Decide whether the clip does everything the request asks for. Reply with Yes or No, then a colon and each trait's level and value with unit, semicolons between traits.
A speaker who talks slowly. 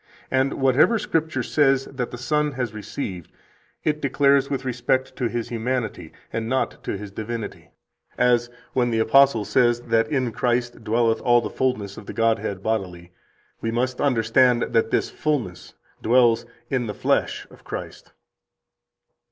No: average, 150 wpm